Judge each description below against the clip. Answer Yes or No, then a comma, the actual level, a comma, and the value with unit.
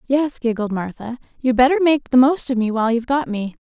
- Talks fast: Yes, fast, 230 wpm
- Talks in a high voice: Yes, very high, 250 Hz